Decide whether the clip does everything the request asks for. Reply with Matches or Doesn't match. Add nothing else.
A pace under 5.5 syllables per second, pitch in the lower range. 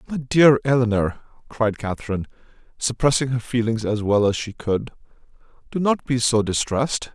Matches